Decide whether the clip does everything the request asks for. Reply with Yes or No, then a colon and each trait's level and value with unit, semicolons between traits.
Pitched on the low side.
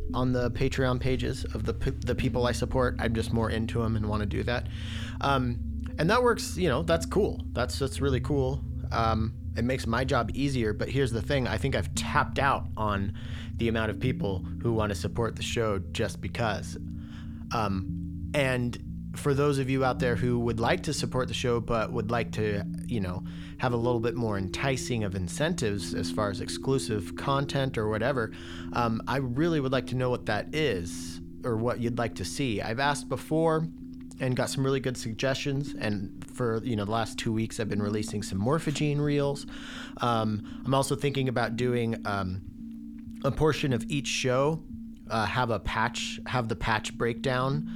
Yes: low, 115 Hz